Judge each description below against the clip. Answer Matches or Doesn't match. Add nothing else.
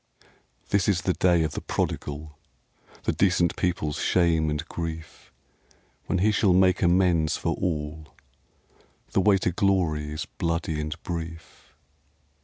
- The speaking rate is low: Matches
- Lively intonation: Doesn't match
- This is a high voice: Doesn't match